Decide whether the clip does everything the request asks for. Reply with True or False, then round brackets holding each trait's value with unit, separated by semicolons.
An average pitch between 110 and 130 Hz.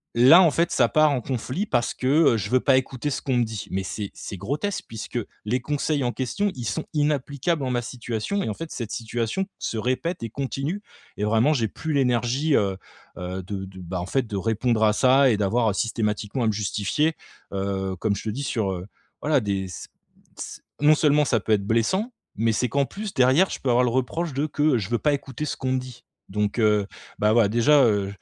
True (120 Hz)